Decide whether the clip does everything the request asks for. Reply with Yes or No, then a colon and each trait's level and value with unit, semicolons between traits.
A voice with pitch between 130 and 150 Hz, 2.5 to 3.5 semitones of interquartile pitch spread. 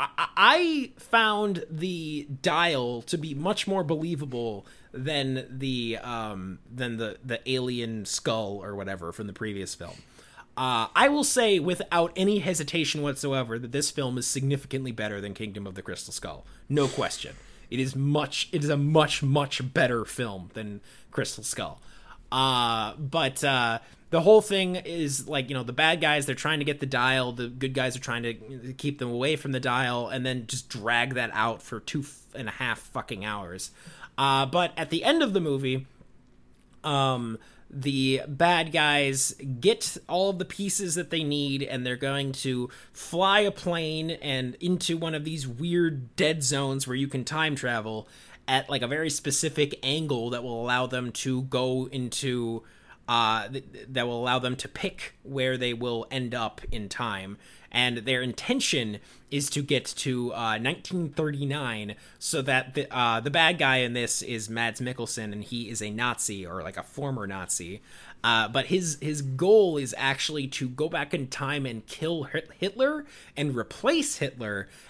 No: low, 135 Hz; average, 4.4 semitones